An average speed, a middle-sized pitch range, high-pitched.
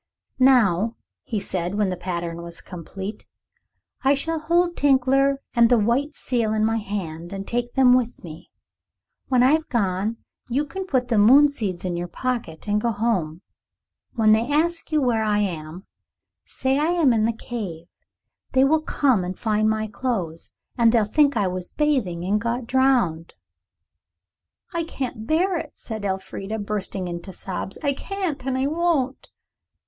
No: average, 165 wpm; wide, 5.8 semitones; high, 230 Hz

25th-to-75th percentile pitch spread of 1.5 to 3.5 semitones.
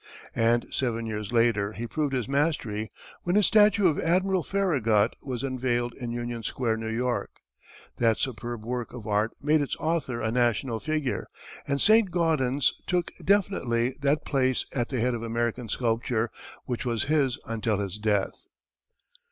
No: average, 4.2 semitones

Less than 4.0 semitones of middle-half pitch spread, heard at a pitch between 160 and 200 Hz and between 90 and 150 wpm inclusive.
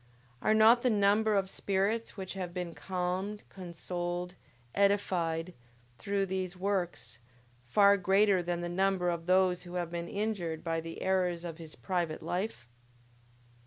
Yes: narrow, 2.4 semitones; medium, 185 Hz; average, 145 wpm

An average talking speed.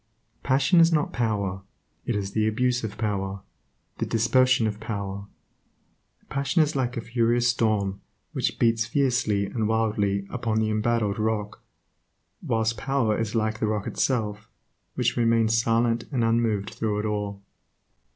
Yes: average, 145 wpm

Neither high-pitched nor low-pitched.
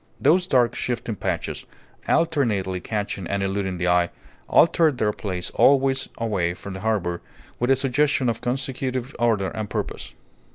No: low, 115 Hz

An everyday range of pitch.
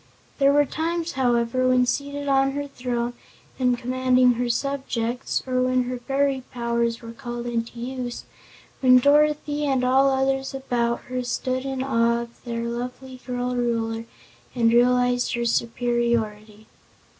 No: narrow, 2.0 semitones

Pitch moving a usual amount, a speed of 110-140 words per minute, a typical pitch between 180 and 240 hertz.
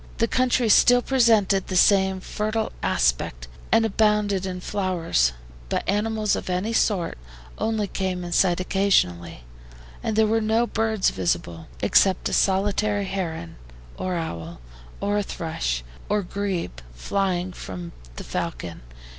Yes: average, 4.2 semitones; slow, 135 wpm; high, 190 Hz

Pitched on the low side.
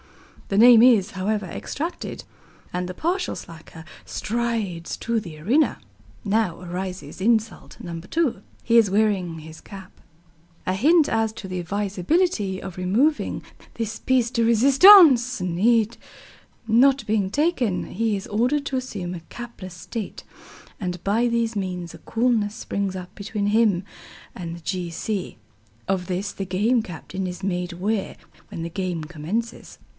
No: high, 205 Hz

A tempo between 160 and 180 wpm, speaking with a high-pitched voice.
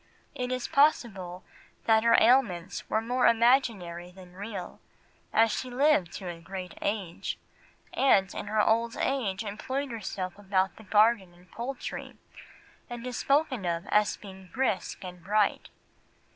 No: average, 145 wpm; high, 210 Hz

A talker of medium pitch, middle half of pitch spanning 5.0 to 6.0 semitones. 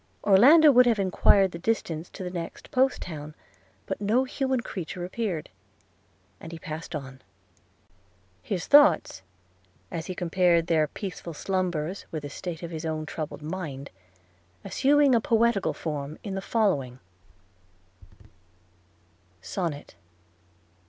Yes: medium, 180 Hz; wide, 5.5 semitones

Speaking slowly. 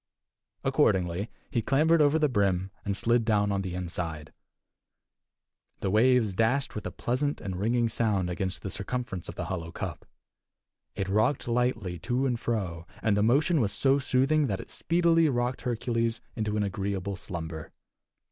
No: average, 160 wpm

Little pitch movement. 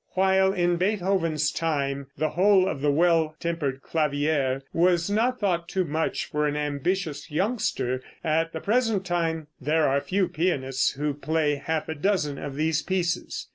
No: average, 4.0 semitones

